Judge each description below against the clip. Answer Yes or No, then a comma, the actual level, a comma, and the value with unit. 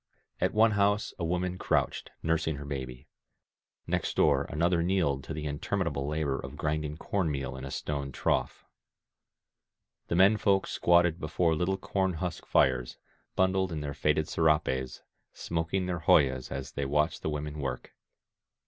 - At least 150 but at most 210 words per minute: Yes, average, 155 wpm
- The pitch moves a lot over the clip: No, average, 4.1 semitones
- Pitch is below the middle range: Yes, very low, 80 Hz